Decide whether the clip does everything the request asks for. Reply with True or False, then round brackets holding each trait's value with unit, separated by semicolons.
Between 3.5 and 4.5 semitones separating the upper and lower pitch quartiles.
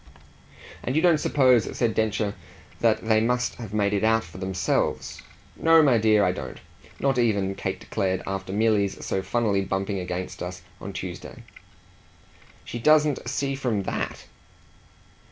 True (4.2 semitones)